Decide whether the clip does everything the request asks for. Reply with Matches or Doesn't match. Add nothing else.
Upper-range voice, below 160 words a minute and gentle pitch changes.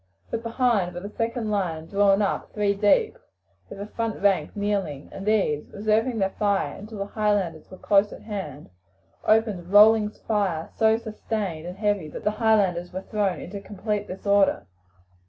Doesn't match